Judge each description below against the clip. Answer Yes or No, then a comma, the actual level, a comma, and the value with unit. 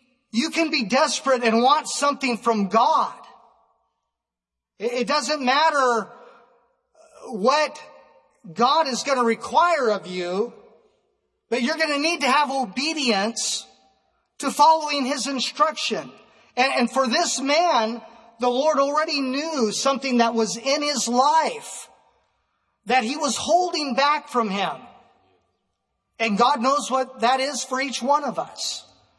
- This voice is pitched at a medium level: No, very high, 265 Hz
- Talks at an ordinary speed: No, slow, 130 wpm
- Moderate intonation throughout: Yes, average, 3.8 semitones